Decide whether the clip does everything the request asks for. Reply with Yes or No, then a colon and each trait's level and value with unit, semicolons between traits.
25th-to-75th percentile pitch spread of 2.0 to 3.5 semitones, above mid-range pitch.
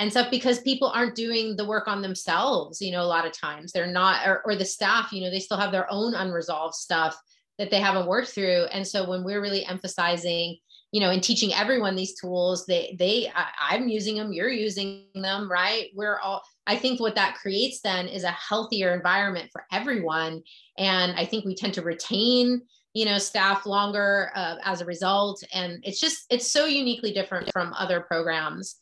Yes: average, 2.8 semitones; high, 195 Hz